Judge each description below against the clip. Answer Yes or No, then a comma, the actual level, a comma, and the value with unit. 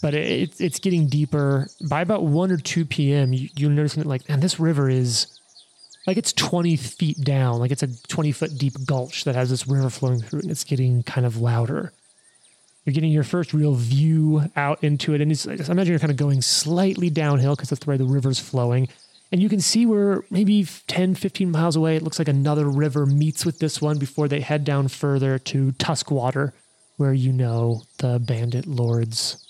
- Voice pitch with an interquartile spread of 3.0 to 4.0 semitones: Yes, average, 3.4 semitones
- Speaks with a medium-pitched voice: Yes, medium, 145 Hz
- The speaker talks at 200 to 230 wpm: Yes, fast, 205 wpm